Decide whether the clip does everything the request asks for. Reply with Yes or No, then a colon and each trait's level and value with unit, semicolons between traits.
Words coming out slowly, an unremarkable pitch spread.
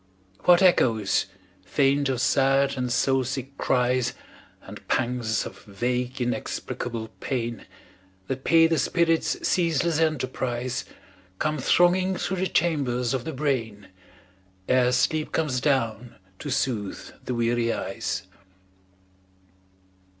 Yes: slow, 115 wpm; average, 4.0 semitones